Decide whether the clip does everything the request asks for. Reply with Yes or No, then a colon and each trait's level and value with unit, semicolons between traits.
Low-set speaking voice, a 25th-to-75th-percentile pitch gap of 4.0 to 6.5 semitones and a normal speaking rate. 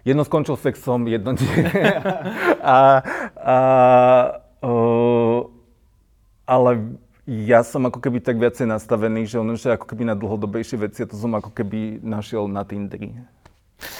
No: low, 120 Hz; narrow, 2.6 semitones; average, 135 wpm